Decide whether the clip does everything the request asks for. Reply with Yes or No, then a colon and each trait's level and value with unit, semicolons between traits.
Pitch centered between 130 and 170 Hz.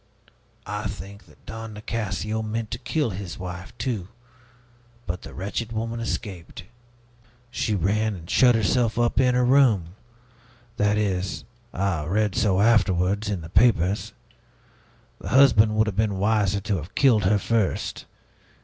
No: low, 105 Hz